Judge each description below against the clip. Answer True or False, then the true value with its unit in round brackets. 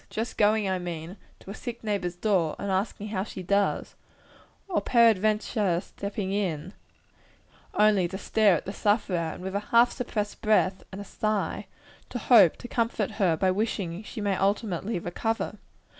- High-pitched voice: True (200 Hz)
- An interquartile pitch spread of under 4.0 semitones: True (2.6 semitones)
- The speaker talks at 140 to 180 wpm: True (165 wpm)